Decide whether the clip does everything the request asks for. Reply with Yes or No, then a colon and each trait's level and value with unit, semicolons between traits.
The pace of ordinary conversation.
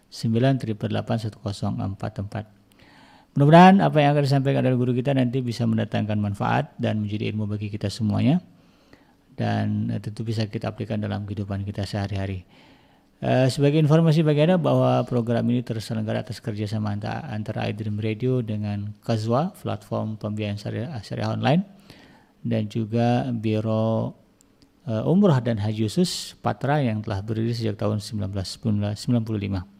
Yes: average, 125 wpm